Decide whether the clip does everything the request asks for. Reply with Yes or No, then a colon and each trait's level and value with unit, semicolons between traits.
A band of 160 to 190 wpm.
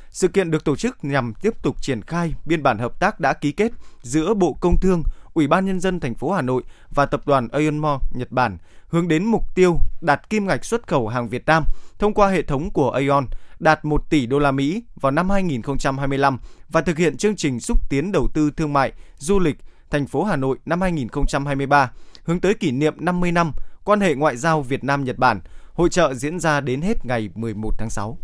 No: average, 225 wpm